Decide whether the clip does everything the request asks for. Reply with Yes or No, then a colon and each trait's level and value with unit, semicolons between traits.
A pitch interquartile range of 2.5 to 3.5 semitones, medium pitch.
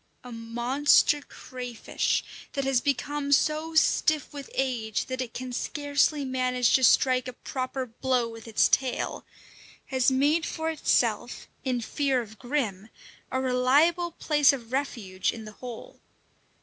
No: average, 2.9 semitones; very high, 260 Hz